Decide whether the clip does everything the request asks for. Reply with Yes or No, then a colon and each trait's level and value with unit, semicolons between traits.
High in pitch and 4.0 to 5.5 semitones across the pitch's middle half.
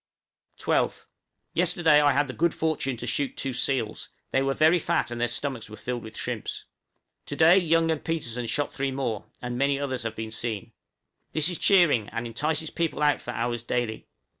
No: low, 135 Hz; average, 4.8 semitones